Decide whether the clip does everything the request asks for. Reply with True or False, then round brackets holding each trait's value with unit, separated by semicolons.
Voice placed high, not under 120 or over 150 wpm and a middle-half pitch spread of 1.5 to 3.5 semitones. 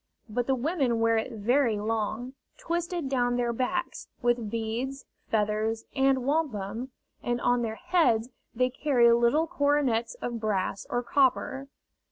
True (245 Hz; 140 wpm; 3.2 semitones)